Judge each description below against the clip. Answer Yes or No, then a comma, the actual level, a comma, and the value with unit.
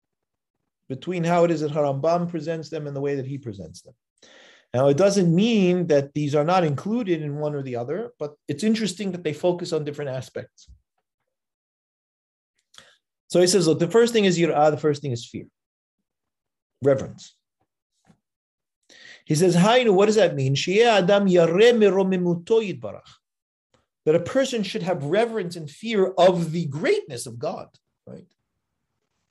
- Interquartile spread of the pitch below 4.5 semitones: No, average, 5.0 semitones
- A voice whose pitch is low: No, medium, 170 Hz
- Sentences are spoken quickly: No, average, 155 wpm